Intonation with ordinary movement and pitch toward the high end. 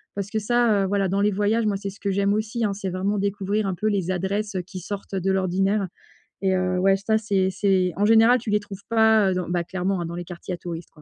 No: narrow, 2.0 semitones; high, 195 Hz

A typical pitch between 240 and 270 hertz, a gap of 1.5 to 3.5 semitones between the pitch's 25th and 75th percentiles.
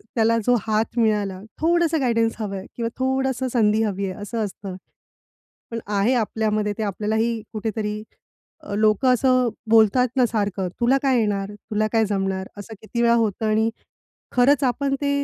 No: high, 220 Hz; average, 2.8 semitones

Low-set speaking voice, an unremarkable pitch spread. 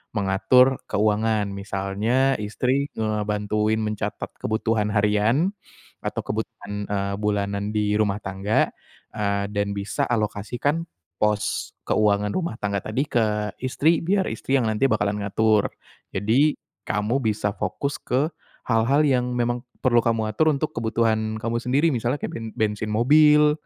Yes: low, 110 Hz; average, 3.2 semitones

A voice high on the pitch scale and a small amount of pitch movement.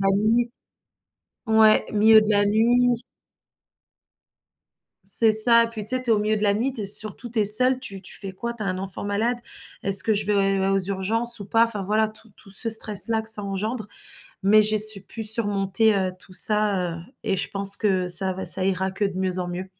Yes: high, 210 Hz; narrow, 2.3 semitones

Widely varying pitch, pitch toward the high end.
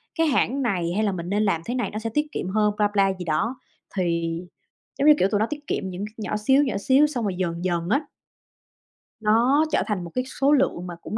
Yes: wide, 6.1 semitones; high, 210 Hz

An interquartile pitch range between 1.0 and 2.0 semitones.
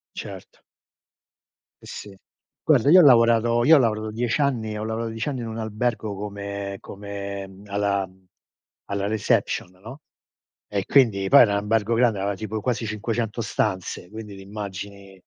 No: narrow, 2.5 semitones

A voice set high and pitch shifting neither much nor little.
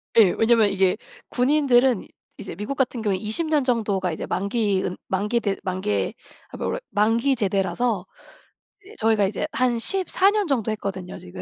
Yes: high, 220 Hz; average, 4.4 semitones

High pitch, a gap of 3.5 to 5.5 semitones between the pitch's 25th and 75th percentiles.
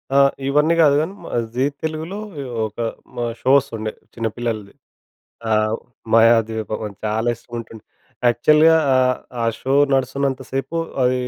No: low, 120 Hz; average, 3.8 semitones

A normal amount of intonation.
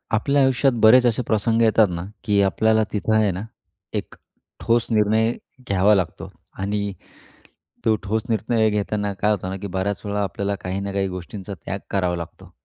No: narrow, 2.1 semitones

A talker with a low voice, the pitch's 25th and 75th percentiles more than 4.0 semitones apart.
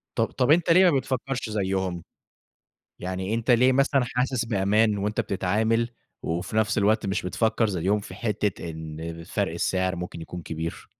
Yes: low, 105 Hz; average, 4.4 semitones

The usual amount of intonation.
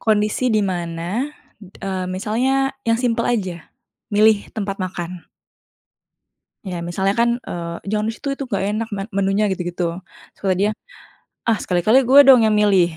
Yes: average, 3.5 semitones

